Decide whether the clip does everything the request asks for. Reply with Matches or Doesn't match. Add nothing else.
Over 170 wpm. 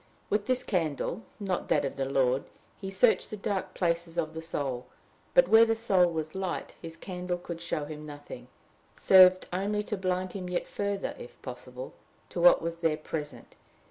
Matches